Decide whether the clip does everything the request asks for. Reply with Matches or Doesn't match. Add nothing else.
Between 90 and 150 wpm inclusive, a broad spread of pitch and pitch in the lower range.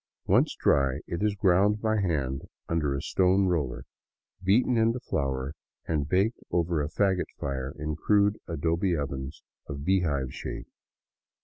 Matches